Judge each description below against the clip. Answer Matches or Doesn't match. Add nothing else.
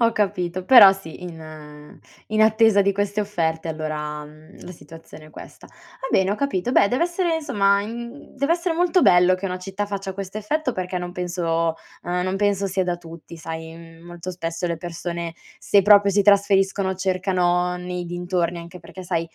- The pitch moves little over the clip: Doesn't match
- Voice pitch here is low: Doesn't match